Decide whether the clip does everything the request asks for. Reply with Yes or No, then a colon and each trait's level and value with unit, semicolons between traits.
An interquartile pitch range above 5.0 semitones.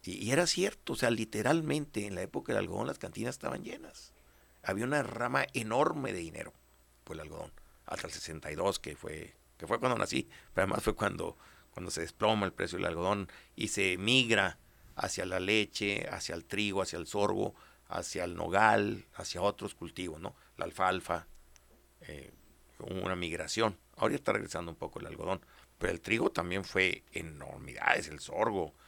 Yes: wide, 5.5 semitones